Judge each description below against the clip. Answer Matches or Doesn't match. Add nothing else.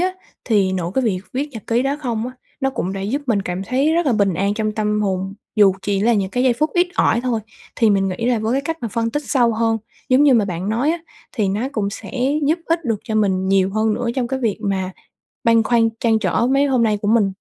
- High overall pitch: Matches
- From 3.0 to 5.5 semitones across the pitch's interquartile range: Matches